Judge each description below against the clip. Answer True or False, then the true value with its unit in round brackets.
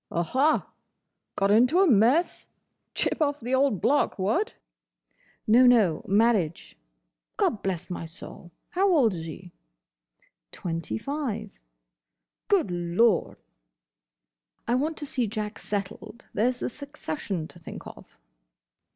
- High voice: True (220 Hz)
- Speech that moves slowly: True (110 wpm)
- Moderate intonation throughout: False (7.1 semitones)